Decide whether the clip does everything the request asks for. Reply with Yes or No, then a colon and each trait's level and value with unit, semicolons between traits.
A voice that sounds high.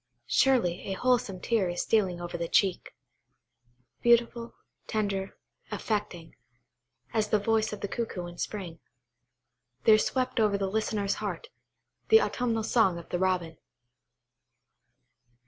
Yes: high, 205 Hz